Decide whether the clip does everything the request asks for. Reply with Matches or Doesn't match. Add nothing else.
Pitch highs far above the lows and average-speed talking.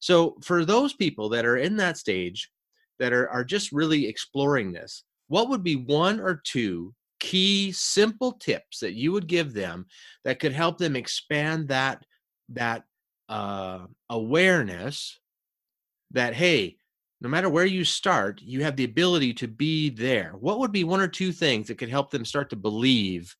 Matches